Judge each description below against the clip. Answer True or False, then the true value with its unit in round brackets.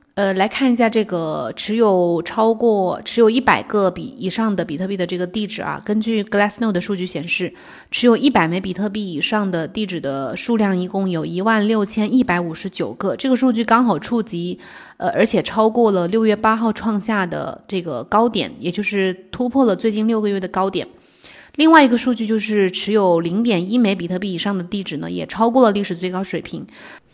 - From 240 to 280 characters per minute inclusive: False (325 characters per minute)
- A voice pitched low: False (205 Hz)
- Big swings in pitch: False (3.6 semitones)